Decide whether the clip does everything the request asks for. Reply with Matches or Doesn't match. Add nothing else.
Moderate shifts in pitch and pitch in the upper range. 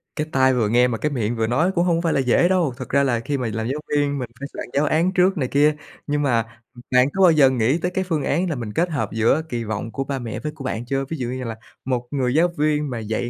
Doesn't match